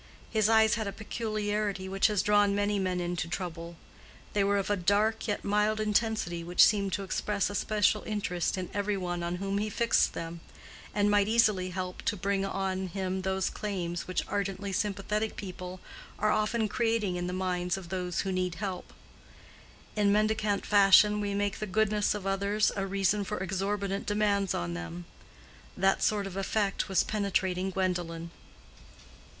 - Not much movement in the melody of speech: Yes, narrow, 2.2 semitones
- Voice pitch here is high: Yes, high, 195 Hz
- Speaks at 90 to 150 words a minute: No, average, 170 wpm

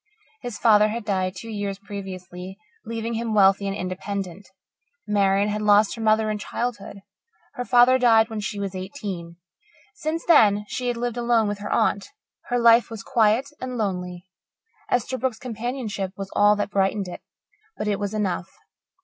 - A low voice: No, high, 210 Hz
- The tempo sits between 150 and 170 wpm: Yes, average, 165 wpm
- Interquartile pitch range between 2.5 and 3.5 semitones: Yes, average, 3.0 semitones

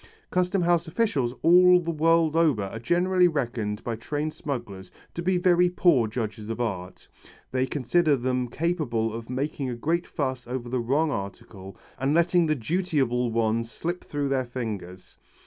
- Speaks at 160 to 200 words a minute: Yes, average, 165 wpm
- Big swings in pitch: Yes, wide, 6.4 semitones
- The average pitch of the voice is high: No, low, 130 Hz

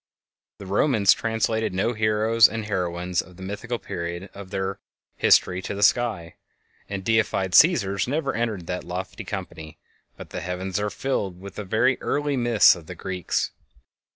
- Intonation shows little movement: No, average, 3.6 semitones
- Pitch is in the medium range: No, low, 100 Hz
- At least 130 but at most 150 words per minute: No, average, 160 wpm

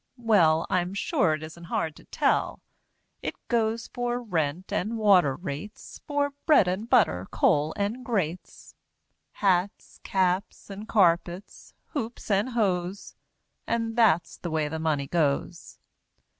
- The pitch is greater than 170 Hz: Yes, high, 190 Hz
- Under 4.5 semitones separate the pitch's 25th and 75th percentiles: No, wide, 5.5 semitones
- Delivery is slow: Yes, slow, 130 wpm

